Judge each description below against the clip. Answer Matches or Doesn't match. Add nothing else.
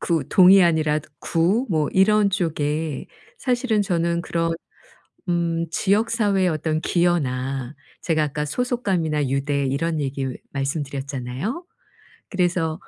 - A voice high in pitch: Doesn't match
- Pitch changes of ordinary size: Matches